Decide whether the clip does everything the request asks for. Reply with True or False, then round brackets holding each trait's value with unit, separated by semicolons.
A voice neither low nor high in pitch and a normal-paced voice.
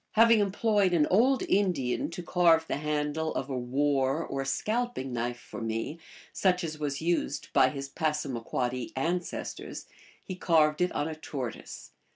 True (155 Hz; 155 wpm)